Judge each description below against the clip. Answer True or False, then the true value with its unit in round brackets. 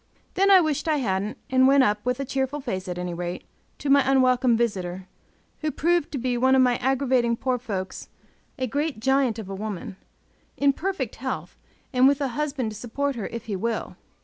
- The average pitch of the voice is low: False (255 Hz)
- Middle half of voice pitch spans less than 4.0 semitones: False (4.3 semitones)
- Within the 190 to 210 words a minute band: True (200 wpm)